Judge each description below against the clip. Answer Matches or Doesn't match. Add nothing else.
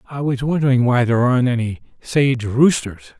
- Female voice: Doesn't match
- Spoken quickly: Doesn't match